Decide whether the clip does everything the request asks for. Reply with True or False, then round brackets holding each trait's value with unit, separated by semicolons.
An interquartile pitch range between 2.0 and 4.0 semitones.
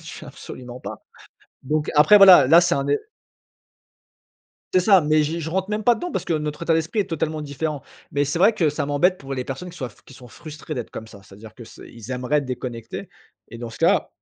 False (4.8 semitones)